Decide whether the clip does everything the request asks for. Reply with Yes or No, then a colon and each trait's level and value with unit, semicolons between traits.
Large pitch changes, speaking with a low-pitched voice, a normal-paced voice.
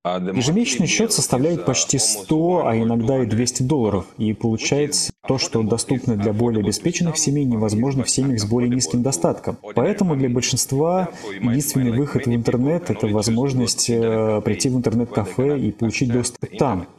No: average, 3.9 semitones; low, 125 Hz; average, 150 wpm